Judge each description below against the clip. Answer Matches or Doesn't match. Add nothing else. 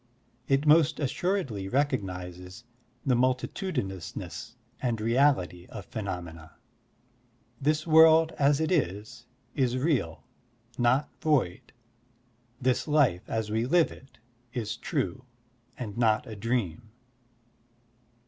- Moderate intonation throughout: Doesn't match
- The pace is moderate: Doesn't match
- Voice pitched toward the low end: Matches